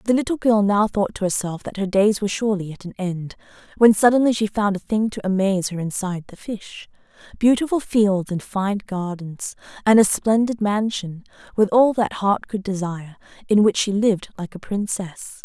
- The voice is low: No, high, 205 Hz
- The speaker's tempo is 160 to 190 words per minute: Yes, average, 185 wpm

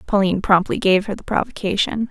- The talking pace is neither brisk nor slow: Yes, average, 170 wpm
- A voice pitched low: No, high, 205 Hz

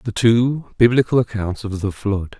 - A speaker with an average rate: Yes, average, 175 wpm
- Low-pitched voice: Yes, low, 110 Hz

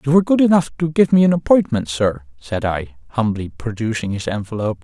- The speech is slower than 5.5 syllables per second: No, 6.1 syllables/s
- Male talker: Yes, male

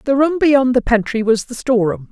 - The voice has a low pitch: No, high, 245 Hz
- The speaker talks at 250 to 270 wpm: No, fast, 225 wpm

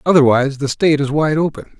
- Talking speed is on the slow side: No, average, 200 wpm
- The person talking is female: No, male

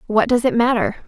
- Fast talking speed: Yes, fast, 225 wpm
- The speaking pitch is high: Yes, high, 235 Hz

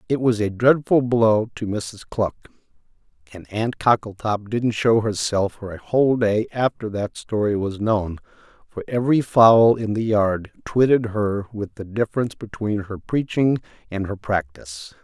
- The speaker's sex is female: No, male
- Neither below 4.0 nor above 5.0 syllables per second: Yes, 4.5 syllables/s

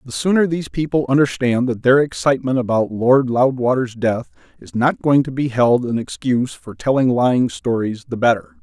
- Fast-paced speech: No, average, 180 wpm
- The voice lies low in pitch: Yes, low, 125 Hz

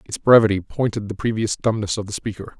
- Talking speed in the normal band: No, fast, 210 wpm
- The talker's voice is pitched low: Yes, low, 105 Hz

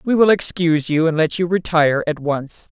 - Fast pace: Yes, fast, 215 wpm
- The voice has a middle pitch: Yes, medium, 165 Hz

